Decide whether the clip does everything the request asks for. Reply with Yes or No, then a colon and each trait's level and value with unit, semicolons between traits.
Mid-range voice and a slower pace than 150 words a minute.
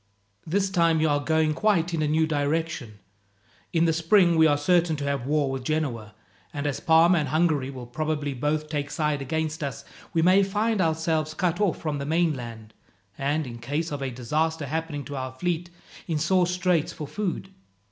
No: medium, 155 Hz; average, 190 wpm